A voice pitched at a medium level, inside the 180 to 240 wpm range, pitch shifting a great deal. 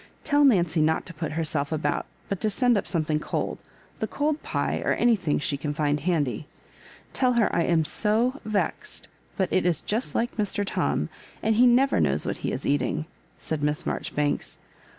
Yes: medium, 175 Hz; average, 190 wpm; wide, 7.2 semitones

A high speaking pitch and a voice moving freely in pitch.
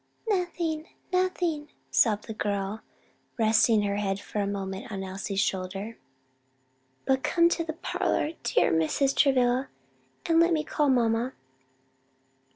Yes: high, 235 Hz; wide, 7.5 semitones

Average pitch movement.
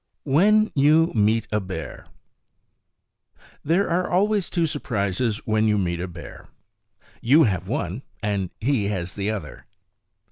No: wide, 8.1 semitones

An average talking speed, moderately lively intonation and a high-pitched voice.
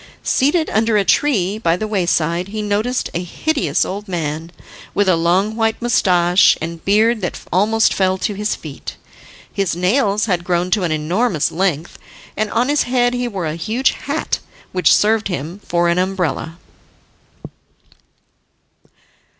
Yes: average, 150 wpm; average, 4.2 semitones; high, 195 Hz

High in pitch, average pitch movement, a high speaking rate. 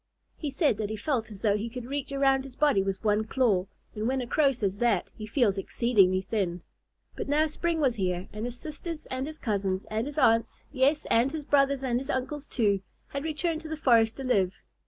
Yes: high, 245 Hz; average, 5.0 semitones; fast, 220 wpm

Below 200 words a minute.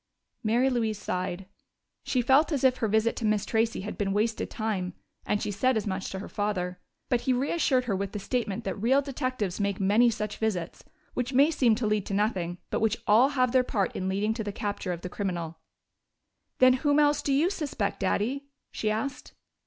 No: fast, 205 wpm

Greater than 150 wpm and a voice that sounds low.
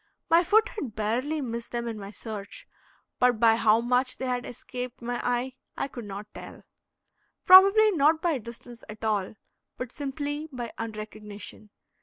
No: average, 160 wpm; high, 245 Hz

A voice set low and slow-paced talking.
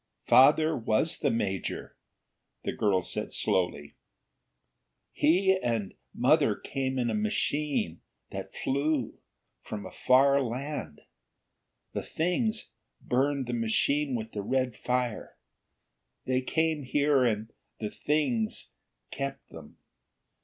Yes: low, 130 Hz; slow, 110 wpm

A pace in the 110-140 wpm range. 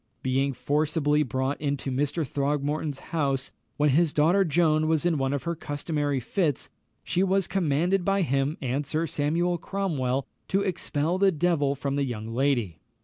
No: average, 160 wpm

